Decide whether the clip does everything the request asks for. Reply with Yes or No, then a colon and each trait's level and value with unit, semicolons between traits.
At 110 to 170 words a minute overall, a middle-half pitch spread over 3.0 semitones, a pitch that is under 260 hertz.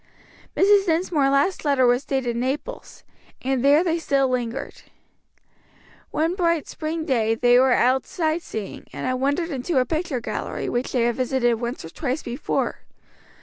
No: average, 160 wpm; average, 4.5 semitones; very high, 270 Hz